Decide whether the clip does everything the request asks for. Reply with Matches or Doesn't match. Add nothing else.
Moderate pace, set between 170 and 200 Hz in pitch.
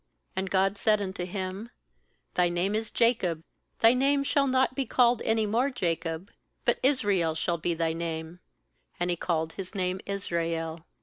Matches